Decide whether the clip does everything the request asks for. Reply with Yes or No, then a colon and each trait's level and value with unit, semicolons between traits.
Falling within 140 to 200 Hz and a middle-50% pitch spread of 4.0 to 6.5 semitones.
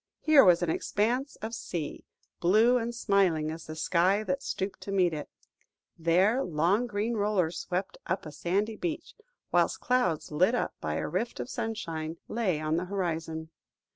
Yes: medium, 185 Hz; average, 5.1 semitones